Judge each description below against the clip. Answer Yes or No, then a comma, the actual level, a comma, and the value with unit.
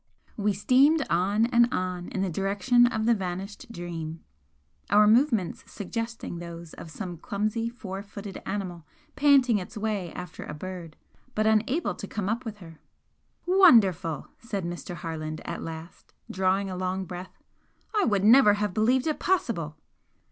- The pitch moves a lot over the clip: No, average, 4.5 semitones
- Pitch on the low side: No, high, 200 Hz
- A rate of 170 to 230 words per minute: No, average, 155 wpm